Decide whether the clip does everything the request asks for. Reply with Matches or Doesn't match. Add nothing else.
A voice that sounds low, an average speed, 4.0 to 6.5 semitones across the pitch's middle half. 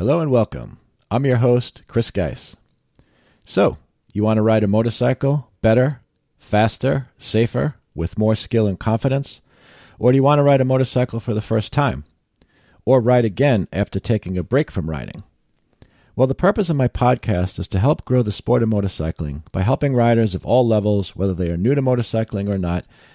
Matches